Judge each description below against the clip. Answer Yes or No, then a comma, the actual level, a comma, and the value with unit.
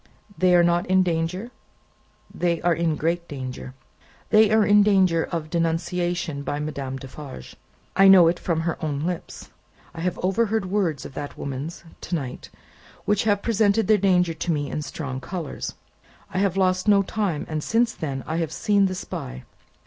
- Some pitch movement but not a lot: Yes, average, 3.9 semitones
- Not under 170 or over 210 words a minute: Yes, average, 175 wpm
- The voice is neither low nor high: Yes, medium, 175 Hz